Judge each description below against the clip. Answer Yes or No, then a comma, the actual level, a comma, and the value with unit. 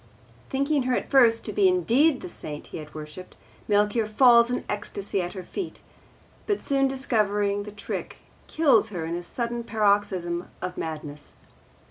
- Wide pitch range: Yes, wide, 6.0 semitones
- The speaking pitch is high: Yes, high, 210 Hz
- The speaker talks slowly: No, average, 160 wpm